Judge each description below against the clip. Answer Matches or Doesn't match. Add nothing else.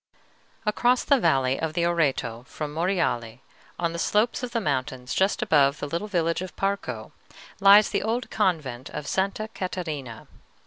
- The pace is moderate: Matches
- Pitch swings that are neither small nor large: Doesn't match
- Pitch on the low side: Doesn't match